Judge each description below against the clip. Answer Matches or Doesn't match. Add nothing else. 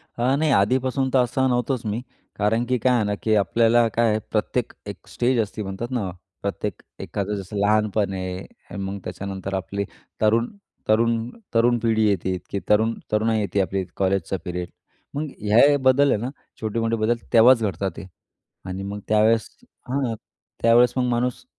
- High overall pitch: Doesn't match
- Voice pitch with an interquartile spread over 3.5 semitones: Doesn't match